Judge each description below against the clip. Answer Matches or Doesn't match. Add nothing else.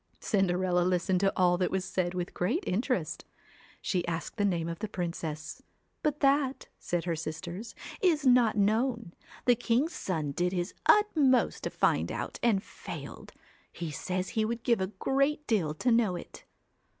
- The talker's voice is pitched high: Matches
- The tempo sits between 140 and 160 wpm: Doesn't match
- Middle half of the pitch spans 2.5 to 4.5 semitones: Doesn't match